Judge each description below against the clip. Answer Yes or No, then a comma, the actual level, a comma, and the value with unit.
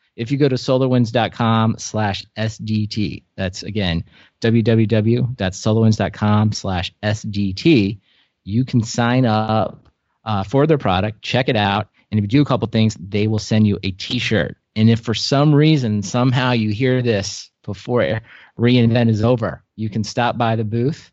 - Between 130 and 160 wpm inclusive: Yes, average, 155 wpm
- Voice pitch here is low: Yes, low, 110 Hz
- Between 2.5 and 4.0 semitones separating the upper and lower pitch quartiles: Yes, average, 2.8 semitones